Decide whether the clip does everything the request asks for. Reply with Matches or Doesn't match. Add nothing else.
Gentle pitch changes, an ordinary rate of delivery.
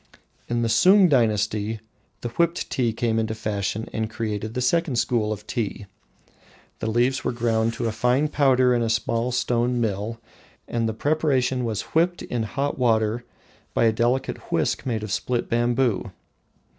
Matches